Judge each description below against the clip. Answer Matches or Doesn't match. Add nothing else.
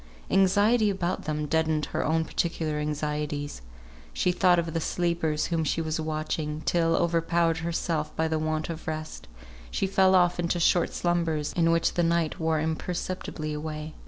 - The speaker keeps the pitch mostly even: Matches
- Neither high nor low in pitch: Matches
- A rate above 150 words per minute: Matches